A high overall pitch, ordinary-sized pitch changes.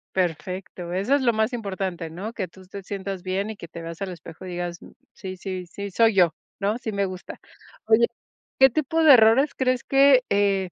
Yes: high, 195 Hz; average, 4.0 semitones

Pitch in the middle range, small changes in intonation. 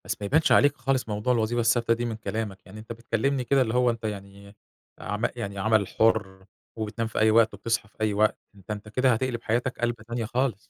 No: low, 110 Hz; narrow, 2.3 semitones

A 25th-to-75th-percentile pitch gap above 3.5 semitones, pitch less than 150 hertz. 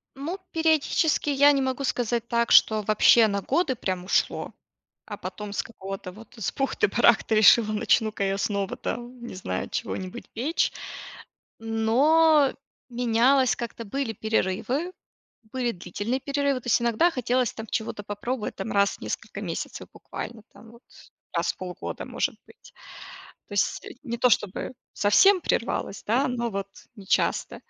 No: average, 4.0 semitones; high, 235 Hz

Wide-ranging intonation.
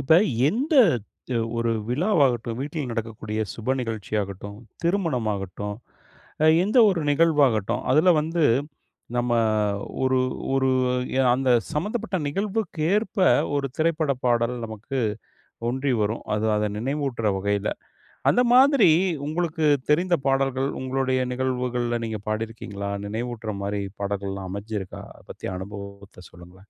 Yes: wide, 6.3 semitones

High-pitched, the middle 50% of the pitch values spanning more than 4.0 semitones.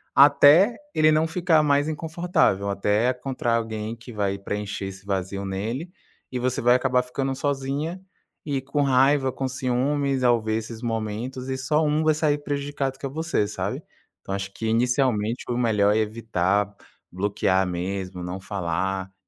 No: low, 125 Hz; wide, 5.6 semitones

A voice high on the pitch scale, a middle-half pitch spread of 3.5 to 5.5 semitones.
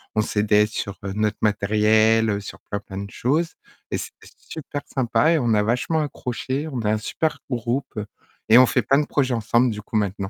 No: low, 110 Hz; average, 3.8 semitones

